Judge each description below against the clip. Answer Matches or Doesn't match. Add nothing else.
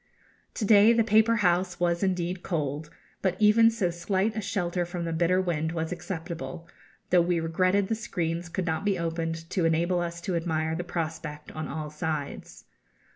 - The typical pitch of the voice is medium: Matches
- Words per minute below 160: Doesn't match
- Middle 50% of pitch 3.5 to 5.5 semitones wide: Doesn't match